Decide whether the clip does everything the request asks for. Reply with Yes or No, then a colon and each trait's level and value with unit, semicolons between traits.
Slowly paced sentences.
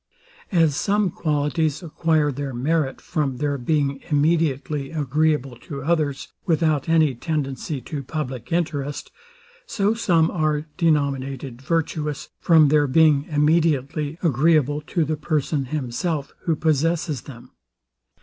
Yes: slow, 120 wpm